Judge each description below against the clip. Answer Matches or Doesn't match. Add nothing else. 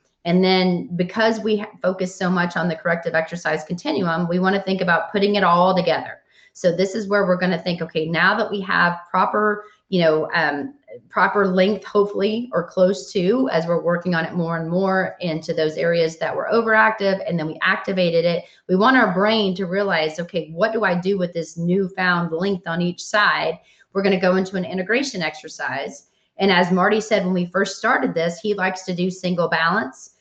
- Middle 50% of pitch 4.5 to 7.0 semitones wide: Doesn't match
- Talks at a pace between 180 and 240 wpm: Matches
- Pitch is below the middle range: Doesn't match